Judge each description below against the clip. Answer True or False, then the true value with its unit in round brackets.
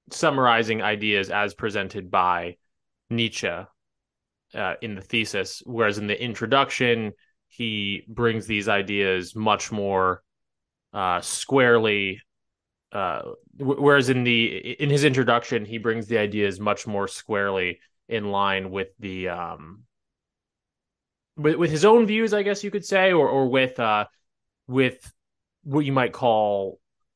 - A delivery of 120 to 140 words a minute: True (135 wpm)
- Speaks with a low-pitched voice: True (110 Hz)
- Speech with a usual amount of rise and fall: True (4.3 semitones)